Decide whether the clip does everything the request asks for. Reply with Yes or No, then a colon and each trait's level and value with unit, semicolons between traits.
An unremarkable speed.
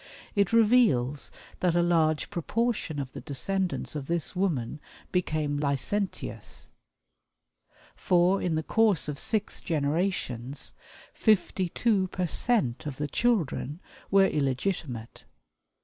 No: slow, 110 wpm